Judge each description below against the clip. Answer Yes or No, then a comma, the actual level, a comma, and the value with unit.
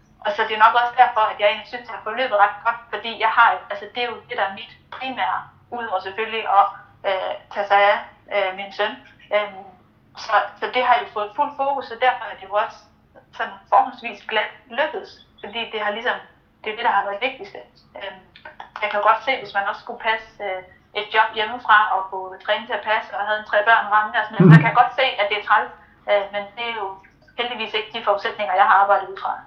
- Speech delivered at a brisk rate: Yes, fast, 240 wpm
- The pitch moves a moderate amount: No, narrow, 2.3 semitones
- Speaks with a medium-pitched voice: No, high, 215 Hz